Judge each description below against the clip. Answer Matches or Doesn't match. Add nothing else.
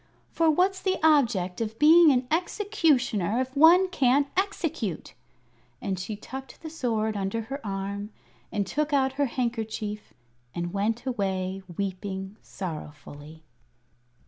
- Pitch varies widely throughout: Matches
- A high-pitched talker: Matches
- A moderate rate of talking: Doesn't match